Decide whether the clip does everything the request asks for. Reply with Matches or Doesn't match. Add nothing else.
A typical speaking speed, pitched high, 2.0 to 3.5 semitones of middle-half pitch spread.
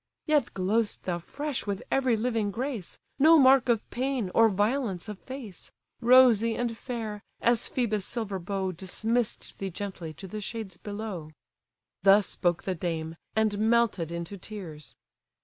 Doesn't match